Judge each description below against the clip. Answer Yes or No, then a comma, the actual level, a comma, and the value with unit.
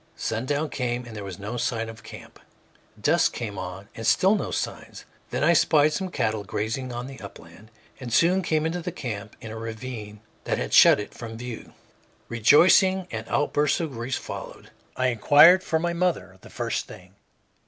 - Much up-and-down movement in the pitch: Yes, wide, 5.8 semitones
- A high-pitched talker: No, low, 120 Hz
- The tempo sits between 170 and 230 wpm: Yes, average, 185 wpm